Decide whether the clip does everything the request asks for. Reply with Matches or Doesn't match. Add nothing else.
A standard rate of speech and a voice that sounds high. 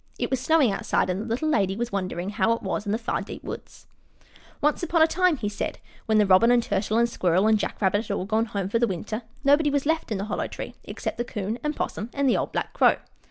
Doesn't match